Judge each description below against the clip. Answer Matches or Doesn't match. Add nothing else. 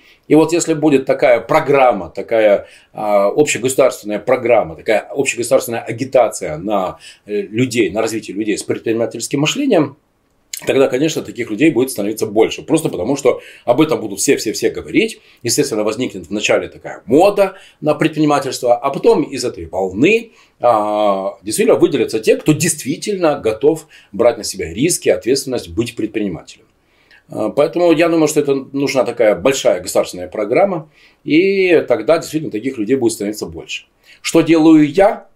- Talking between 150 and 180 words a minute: Doesn't match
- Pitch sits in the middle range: Matches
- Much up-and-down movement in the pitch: Matches